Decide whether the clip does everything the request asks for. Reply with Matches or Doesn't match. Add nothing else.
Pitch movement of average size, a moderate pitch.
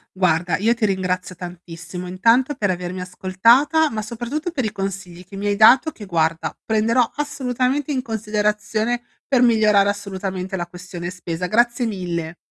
Doesn't match